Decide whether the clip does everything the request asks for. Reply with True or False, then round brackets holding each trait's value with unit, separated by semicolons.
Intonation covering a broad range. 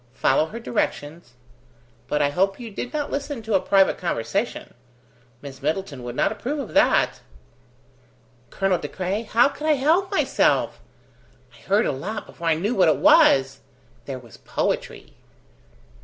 True (8.0 semitones)